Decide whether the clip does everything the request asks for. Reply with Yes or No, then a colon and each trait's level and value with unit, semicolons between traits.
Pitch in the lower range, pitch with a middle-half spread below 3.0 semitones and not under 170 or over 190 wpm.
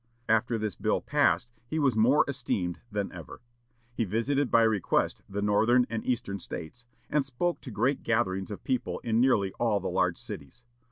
No: low, 115 Hz; average, 3.6 semitones; average, 175 wpm